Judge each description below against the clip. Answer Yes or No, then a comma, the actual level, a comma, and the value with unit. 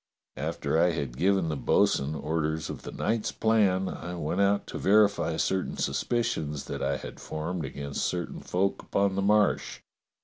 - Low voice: Yes, very low, 90 Hz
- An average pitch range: Yes, average, 4.5 semitones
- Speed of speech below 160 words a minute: No, average, 165 wpm